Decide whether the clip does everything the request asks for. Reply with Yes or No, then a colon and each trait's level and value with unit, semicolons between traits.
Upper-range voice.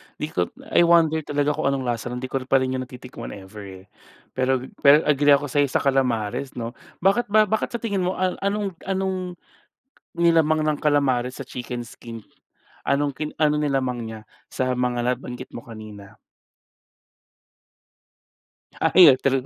No: low, 135 Hz